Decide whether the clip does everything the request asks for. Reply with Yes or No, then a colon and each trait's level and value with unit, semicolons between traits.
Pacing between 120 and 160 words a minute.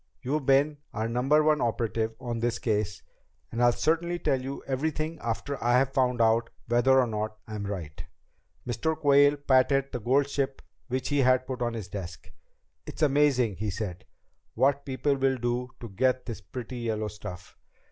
No: average, 170 wpm